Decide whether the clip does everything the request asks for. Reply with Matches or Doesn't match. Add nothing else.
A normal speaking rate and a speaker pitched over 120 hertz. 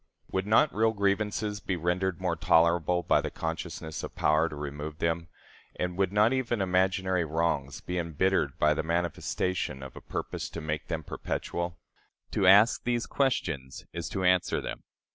Doesn't match